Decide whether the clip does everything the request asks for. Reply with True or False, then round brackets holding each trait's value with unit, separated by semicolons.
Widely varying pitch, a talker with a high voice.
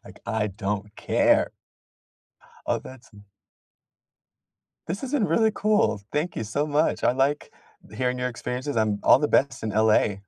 False (5.7 semitones; 125 Hz)